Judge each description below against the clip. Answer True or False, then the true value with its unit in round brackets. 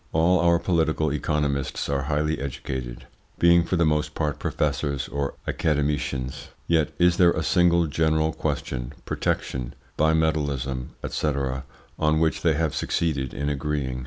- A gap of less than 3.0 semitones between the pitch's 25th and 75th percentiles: True (2.6 semitones)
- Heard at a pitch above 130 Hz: False (75 Hz)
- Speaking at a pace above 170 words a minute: False (135 wpm)